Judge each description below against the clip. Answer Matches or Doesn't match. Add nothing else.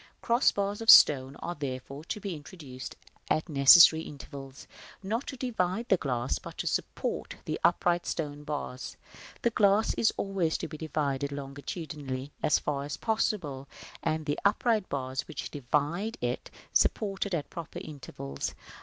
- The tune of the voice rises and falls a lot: Matches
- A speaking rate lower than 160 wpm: Matches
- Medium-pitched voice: Matches